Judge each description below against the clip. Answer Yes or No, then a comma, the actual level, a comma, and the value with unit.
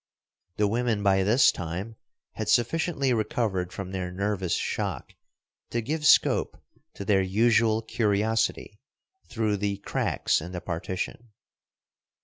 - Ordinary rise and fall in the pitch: Yes, average, 3.3 semitones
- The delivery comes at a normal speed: No, slow, 125 wpm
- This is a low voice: Yes, low, 105 Hz